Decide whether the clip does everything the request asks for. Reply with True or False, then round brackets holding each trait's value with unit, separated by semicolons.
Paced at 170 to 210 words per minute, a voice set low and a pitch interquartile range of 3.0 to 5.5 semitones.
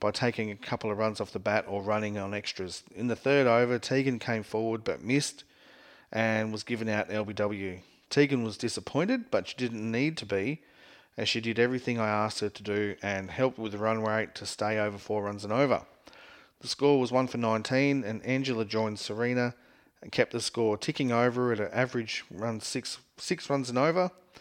True (205 wpm; 115 Hz; 3.3 semitones)